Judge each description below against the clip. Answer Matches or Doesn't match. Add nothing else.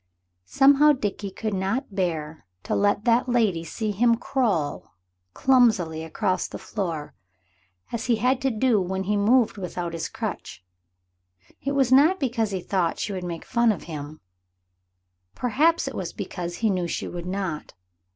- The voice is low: Doesn't match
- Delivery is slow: Doesn't match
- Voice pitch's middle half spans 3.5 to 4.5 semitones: Doesn't match